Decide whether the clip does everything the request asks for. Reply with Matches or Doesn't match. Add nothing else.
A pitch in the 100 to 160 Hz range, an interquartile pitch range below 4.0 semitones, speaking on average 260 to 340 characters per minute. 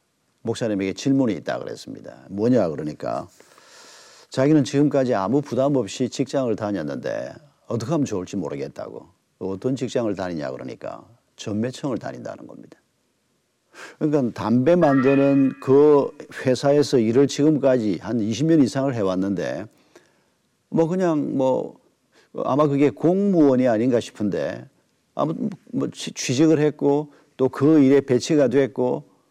Matches